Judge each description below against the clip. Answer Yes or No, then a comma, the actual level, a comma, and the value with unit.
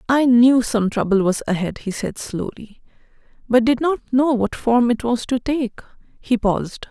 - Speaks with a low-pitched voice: No, high, 240 Hz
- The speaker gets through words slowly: No, average, 180 wpm